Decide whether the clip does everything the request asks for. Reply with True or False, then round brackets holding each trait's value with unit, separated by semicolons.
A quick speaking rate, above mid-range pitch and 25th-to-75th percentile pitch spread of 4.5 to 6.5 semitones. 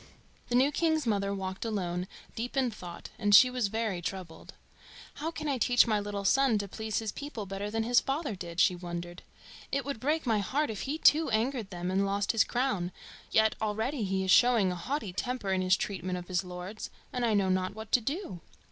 True (215 wpm; 215 Hz; 4.9 semitones)